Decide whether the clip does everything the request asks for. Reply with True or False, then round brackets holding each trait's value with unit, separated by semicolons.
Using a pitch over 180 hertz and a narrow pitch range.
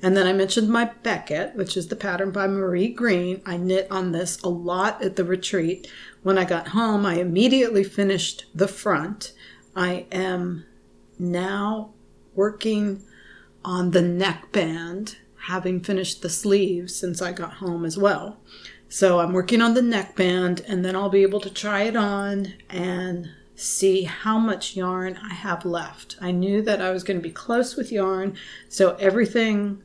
True (190 Hz; 2.1 semitones)